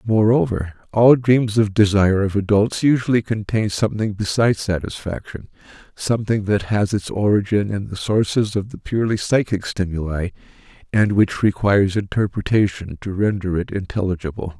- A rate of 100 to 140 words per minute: Yes, slow, 135 wpm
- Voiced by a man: Yes, male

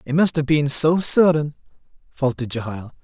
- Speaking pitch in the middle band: Yes, medium, 145 Hz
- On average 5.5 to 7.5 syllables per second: No, 5.2 syllables/s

